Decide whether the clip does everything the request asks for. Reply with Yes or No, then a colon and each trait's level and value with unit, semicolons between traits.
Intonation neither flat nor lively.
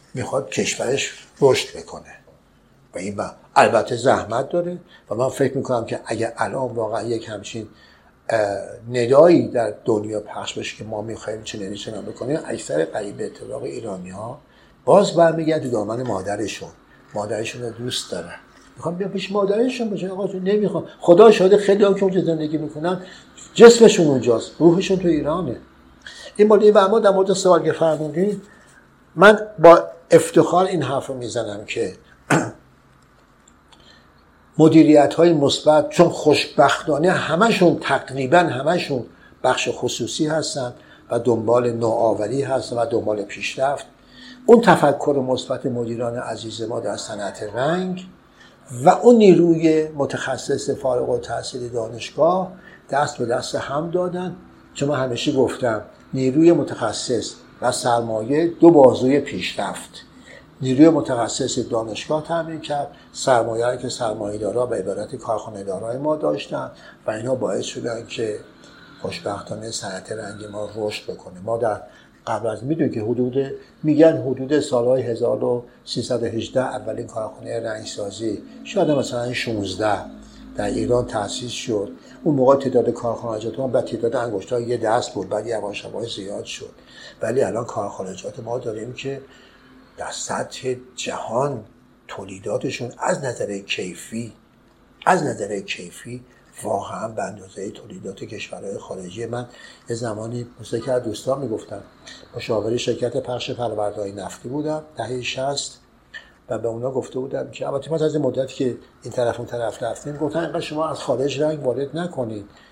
No: wide, 5.8 semitones